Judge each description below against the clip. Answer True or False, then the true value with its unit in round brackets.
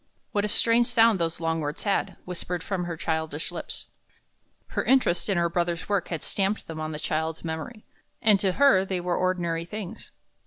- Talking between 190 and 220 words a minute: True (195 wpm)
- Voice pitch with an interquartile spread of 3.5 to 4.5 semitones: True (3.8 semitones)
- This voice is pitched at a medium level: True (175 Hz)